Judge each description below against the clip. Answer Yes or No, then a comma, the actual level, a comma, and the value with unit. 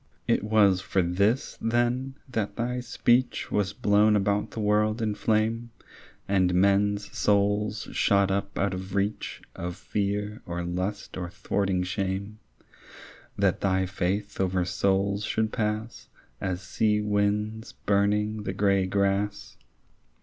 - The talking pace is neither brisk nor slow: No, slow, 130 wpm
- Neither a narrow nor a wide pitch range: No, narrow, 1.8 semitones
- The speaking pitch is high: No, low, 100 Hz